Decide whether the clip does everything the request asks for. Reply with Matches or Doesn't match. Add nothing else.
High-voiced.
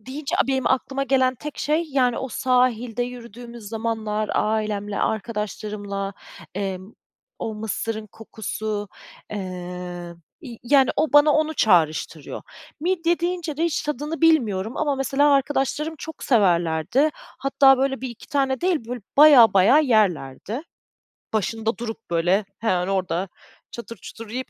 Matches